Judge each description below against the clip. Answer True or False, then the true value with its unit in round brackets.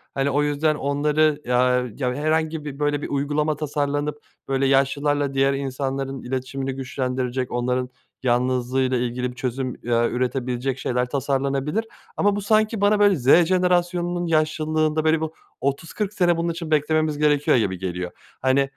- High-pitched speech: False (140 Hz)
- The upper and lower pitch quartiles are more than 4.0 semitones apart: False (3.3 semitones)